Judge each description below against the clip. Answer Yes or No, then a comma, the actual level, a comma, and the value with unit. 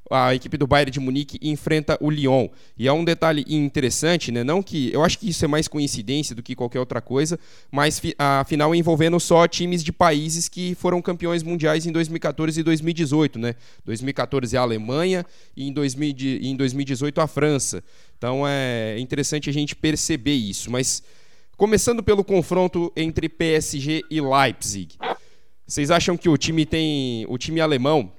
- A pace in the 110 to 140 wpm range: No, average, 165 wpm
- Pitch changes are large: No, average, 3.7 semitones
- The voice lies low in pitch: No, medium, 150 Hz